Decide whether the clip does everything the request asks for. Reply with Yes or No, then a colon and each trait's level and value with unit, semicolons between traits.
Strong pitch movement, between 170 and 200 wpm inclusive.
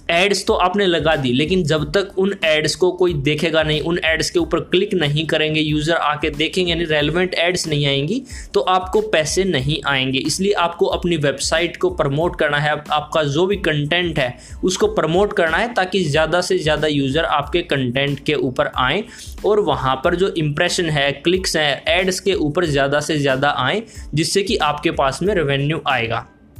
No: average, 3.6 semitones; average, 185 wpm